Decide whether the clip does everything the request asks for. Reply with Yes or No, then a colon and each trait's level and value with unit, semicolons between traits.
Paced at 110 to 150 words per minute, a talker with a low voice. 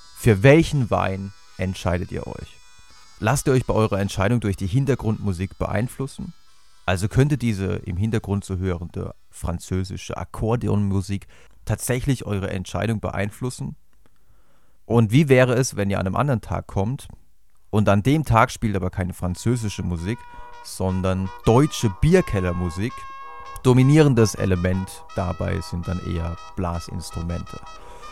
Yes: slow, 125 wpm; low, 100 Hz